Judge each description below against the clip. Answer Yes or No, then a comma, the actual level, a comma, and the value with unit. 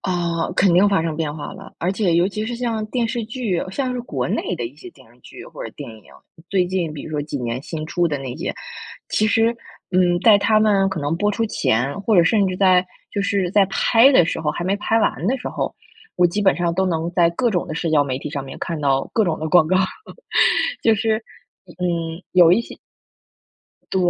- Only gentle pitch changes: No, average, 4.6 semitones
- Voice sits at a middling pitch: Yes, medium, 180 Hz